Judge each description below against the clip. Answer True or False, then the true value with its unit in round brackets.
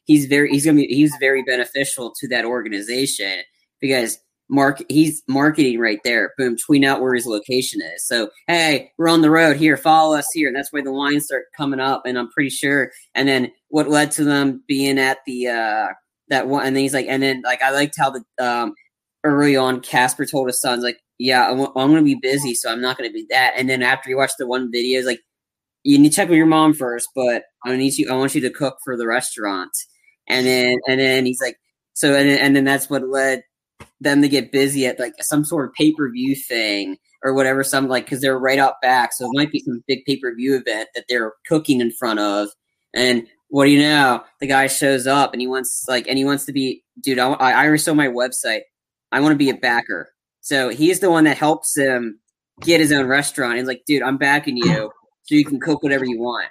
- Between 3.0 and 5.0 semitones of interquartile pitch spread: False (2.5 semitones)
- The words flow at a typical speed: False (235 wpm)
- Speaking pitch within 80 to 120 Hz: False (135 Hz)